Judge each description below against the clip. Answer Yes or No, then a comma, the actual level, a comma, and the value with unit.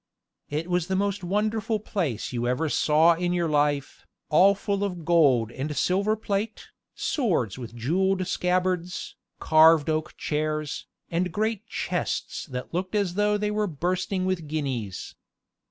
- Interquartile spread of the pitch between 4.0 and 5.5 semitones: Yes, average, 4.6 semitones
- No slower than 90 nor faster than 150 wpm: Yes, average, 145 wpm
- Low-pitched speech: No, medium, 175 Hz